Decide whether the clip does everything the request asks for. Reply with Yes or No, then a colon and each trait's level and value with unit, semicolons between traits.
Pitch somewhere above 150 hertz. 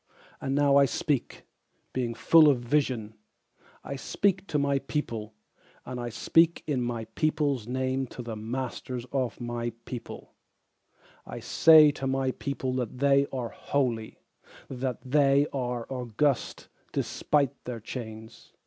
No: low, 130 Hz